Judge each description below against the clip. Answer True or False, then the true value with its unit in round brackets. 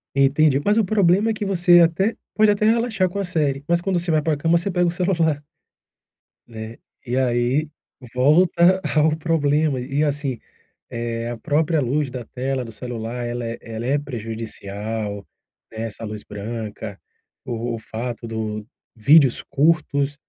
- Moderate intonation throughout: False (6.4 semitones)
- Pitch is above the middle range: False (140 Hz)